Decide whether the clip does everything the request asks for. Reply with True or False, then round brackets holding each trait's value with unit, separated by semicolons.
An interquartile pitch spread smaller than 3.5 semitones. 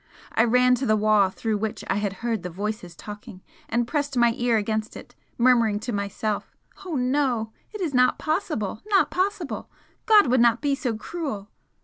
False (4.4 semitones)